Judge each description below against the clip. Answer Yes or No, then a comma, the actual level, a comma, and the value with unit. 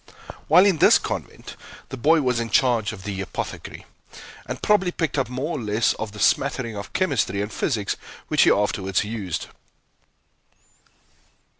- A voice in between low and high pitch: No, low, 115 Hz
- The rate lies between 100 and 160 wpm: Yes, average, 155 wpm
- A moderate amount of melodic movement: No, wide, 5.8 semitones